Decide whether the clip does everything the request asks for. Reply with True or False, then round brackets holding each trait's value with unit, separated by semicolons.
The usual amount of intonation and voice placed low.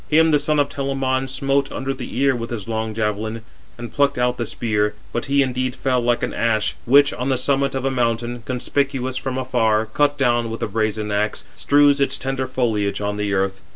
True (3.5 semitones; 125 Hz)